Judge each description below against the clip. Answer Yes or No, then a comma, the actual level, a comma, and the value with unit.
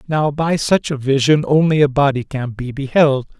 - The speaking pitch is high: No, medium, 140 Hz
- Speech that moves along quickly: No, average, 195 wpm